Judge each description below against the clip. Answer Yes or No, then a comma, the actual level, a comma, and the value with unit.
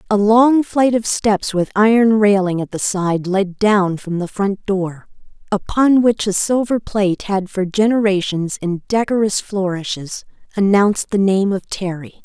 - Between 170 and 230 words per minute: No, average, 160 wpm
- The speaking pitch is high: Yes, high, 200 Hz